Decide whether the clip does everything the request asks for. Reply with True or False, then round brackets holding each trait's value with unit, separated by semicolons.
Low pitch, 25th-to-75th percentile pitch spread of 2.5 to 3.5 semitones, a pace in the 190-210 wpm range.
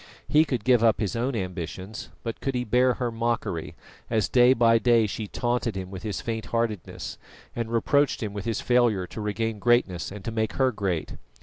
True (115 Hz; 2.9 semitones; 200 wpm)